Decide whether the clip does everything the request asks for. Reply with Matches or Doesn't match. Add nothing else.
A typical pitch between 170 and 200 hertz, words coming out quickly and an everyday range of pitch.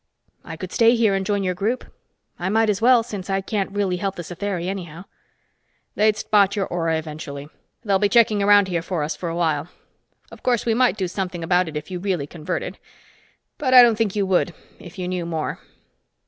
Matches